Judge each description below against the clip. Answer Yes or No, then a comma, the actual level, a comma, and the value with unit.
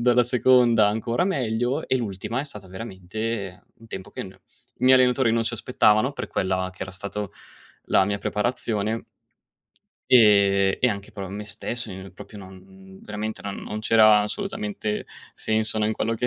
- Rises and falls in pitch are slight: No, average, 3.4 semitones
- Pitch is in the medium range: No, low, 110 Hz